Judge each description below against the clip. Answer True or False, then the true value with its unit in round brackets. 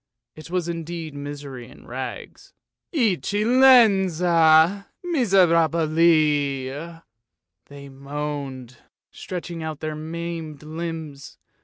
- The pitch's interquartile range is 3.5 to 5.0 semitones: False (3.0 semitones)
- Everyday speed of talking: False (85 wpm)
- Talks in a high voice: False (160 Hz)